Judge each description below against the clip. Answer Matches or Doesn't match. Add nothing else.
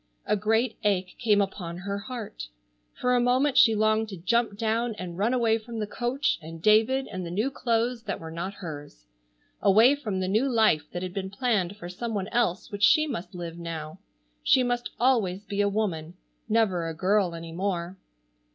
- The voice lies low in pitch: Doesn't match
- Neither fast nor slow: Matches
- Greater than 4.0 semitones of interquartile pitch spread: Matches